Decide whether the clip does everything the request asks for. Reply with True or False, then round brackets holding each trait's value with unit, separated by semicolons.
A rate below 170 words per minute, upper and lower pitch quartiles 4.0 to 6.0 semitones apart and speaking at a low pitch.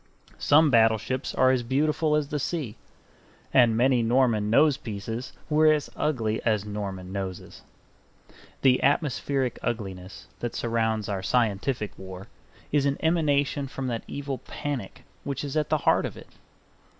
True (140 wpm; 4.8 semitones; 125 Hz)